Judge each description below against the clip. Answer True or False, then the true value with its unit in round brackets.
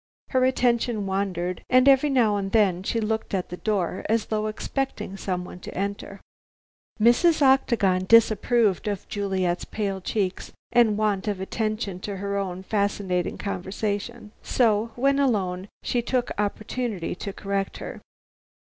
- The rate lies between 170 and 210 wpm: False (145 wpm)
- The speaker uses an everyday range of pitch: True (3.3 semitones)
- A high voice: True (205 Hz)